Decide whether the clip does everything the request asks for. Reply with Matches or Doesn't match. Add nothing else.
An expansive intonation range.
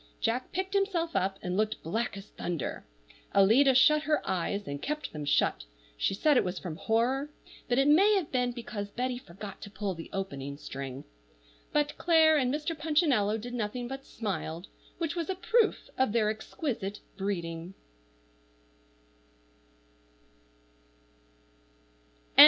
Matches